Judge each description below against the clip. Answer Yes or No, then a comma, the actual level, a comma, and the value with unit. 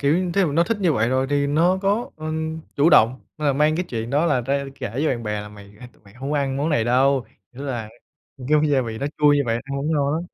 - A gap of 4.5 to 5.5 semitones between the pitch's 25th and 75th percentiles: No, average, 4.1 semitones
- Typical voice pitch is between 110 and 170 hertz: Yes, medium, 140 Hz